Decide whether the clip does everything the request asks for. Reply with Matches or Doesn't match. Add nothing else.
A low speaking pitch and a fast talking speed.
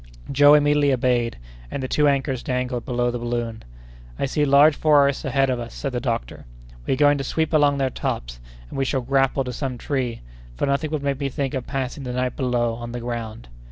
Matches